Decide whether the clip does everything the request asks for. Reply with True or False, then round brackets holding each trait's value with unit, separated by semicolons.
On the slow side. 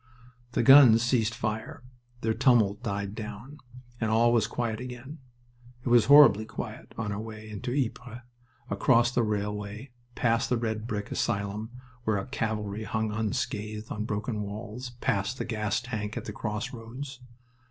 False (155 wpm)